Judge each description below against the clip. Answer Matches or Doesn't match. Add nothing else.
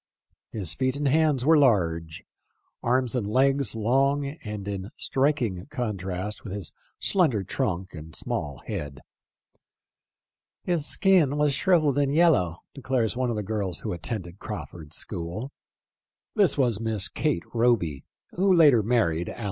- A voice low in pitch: Matches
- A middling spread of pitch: Doesn't match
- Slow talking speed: Matches